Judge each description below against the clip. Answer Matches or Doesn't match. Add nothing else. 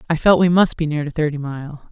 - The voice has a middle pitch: Matches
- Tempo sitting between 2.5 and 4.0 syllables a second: Doesn't match